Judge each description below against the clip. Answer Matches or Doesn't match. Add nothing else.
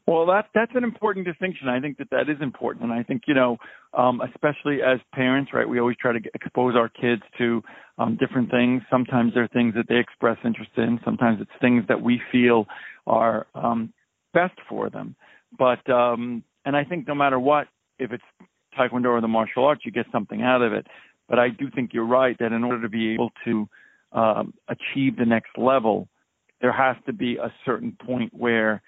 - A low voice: Matches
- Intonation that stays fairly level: Matches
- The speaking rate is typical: Doesn't match